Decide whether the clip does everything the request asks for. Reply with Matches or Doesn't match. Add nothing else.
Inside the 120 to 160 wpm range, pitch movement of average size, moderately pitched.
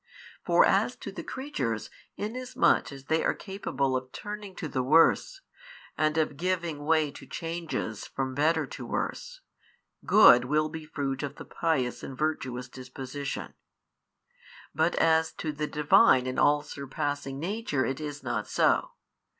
Matches